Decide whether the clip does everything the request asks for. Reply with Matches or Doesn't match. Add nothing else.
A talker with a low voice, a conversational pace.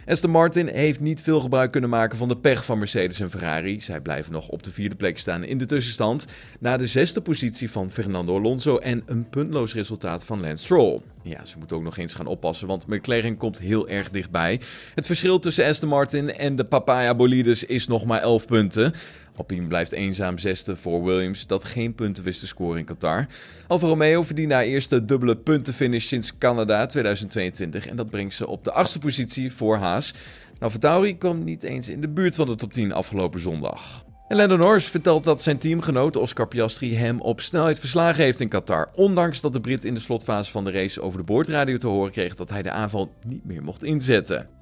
Doesn't match